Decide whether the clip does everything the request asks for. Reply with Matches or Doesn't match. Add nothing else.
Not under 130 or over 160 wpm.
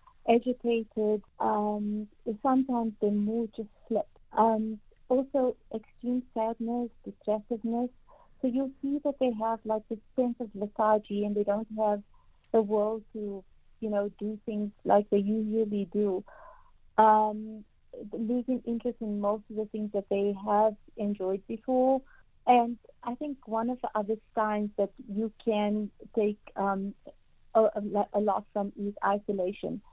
Matches